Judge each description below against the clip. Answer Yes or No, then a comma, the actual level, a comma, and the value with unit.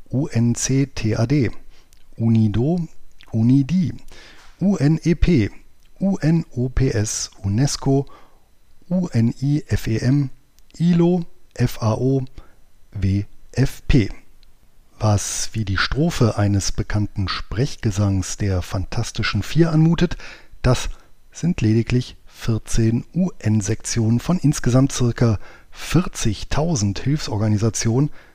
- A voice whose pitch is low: Yes, low, 115 Hz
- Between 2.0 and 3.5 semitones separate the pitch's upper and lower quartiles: No, average, 5.2 semitones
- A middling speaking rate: No, slow, 65 wpm